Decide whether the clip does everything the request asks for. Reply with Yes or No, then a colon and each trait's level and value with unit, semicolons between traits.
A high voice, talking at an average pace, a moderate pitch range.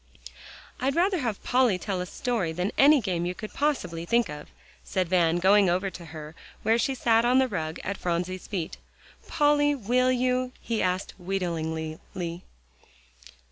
No: high, 195 Hz; average, 160 wpm; wide, 6.4 semitones